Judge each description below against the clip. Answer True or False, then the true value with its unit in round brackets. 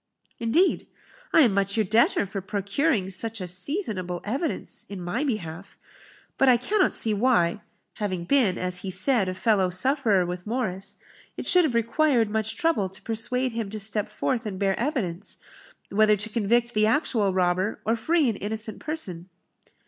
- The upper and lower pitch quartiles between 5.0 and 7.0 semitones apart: False (4.2 semitones)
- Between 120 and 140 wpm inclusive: False (170 wpm)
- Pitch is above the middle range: True (215 Hz)